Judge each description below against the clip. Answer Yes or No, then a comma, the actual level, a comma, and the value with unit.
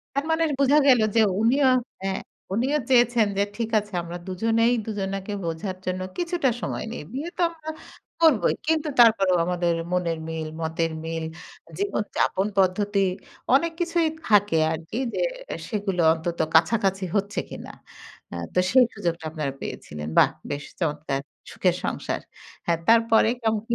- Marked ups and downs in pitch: Yes, wide, 6.0 semitones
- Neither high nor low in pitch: No, high, 205 Hz